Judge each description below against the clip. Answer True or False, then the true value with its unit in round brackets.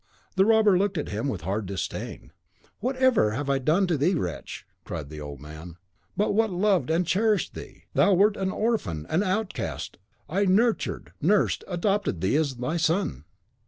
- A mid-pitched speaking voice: True (175 Hz)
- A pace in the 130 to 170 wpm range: False (180 wpm)